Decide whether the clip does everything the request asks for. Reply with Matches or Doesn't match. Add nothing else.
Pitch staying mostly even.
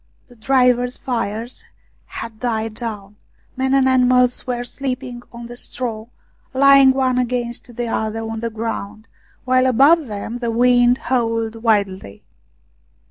Matches